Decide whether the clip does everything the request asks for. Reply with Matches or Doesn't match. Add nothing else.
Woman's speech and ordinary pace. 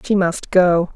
Matches